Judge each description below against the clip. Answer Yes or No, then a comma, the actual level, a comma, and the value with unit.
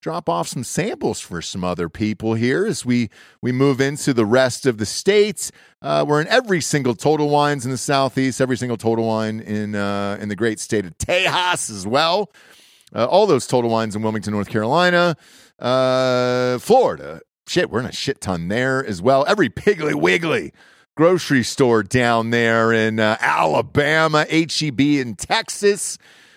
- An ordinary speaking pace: Yes, average, 175 wpm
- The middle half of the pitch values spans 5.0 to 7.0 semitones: Yes, average, 5.3 semitones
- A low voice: Yes, low, 125 Hz